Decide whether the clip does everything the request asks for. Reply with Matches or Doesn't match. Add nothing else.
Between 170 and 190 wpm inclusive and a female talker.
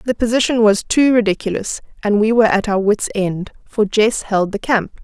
Doesn't match